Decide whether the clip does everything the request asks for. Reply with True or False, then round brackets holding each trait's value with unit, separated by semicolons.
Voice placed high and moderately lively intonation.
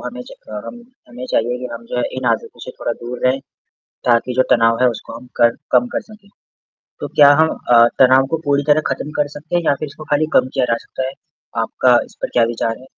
False (130 Hz; 3.7 semitones)